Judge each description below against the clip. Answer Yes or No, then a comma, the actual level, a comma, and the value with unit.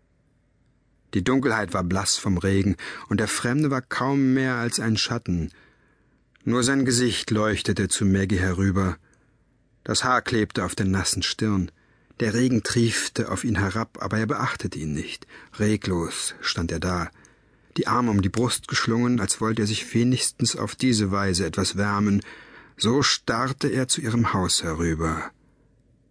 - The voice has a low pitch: Yes, low, 110 Hz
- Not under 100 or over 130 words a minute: No, average, 155 wpm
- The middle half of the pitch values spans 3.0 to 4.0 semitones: No, average, 4.4 semitones